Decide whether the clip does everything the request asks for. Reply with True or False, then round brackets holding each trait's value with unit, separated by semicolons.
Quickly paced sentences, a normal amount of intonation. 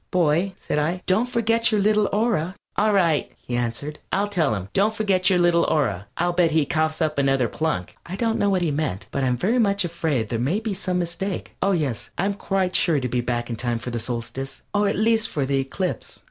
False (235 wpm; 6.6 semitones)